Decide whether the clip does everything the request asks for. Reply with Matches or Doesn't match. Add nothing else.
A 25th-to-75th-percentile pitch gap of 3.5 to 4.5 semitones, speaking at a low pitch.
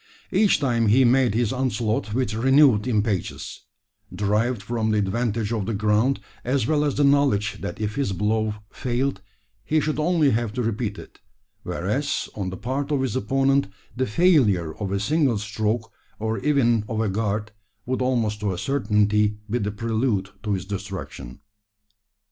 Matches